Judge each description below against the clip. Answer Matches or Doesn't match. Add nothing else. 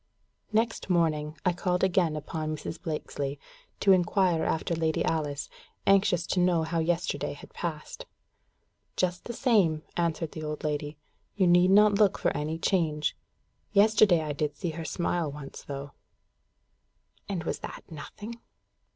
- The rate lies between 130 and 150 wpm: Matches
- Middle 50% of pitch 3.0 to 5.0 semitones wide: Matches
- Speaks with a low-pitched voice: Doesn't match